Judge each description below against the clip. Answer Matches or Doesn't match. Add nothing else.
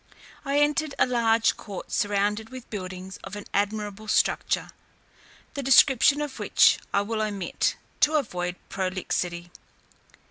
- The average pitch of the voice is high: Matches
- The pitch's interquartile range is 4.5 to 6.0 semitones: Matches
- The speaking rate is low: Matches